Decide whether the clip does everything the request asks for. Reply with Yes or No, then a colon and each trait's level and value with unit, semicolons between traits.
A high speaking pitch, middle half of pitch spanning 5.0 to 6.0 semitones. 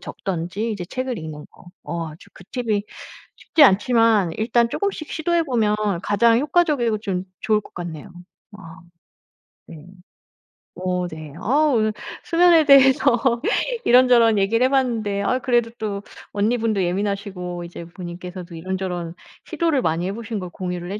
Yes: high, 210 Hz; average, 5.3 semitones